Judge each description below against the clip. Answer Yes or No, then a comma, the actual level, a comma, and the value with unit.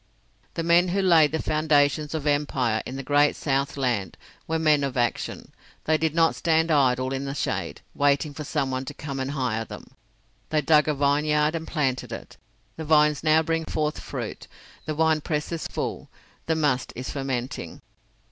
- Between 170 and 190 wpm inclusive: Yes, average, 175 wpm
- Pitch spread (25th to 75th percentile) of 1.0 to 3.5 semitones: Yes, average, 2.7 semitones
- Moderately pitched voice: Yes, medium, 150 Hz